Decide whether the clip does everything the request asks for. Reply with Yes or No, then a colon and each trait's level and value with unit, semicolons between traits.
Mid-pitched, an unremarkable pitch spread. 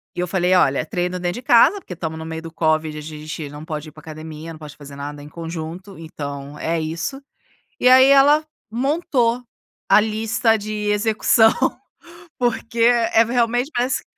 No: medium, 175 Hz; wide, 6.8 semitones